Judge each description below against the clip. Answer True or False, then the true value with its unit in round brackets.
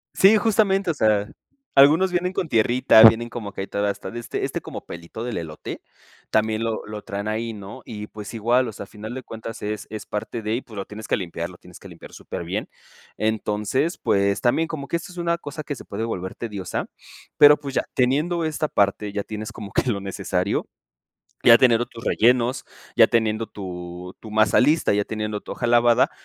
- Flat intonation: False (4.2 semitones)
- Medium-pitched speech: False (110 Hz)